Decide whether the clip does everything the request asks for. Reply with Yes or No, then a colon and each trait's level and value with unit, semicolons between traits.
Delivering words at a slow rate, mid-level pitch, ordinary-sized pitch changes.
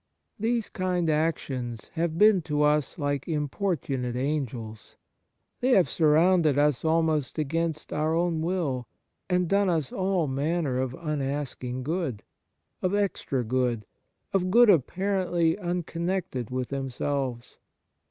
Yes: slow, 125 wpm; medium, 155 Hz; average, 4.9 semitones